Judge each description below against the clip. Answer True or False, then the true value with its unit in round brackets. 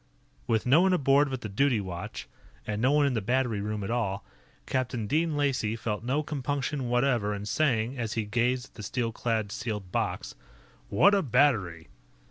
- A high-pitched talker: False (120 Hz)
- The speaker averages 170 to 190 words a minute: True (185 wpm)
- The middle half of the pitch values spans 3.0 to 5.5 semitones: True (4.6 semitones)